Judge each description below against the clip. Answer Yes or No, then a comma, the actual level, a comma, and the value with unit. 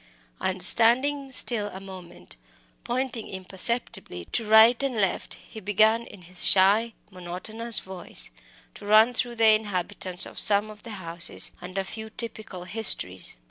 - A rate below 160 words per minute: Yes, average, 145 wpm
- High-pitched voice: Yes, high, 210 Hz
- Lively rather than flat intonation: No, average, 3.6 semitones